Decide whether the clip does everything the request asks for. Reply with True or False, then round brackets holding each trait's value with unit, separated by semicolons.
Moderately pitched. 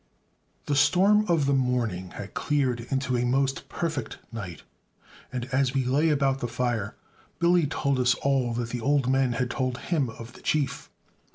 False (130 Hz)